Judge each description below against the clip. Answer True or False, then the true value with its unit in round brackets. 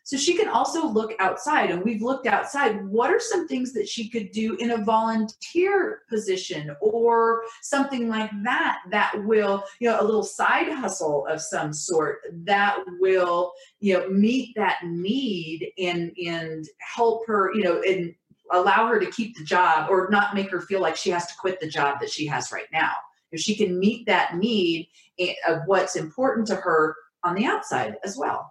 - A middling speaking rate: True (190 wpm)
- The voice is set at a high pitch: True (200 Hz)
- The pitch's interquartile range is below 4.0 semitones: False (4.5 semitones)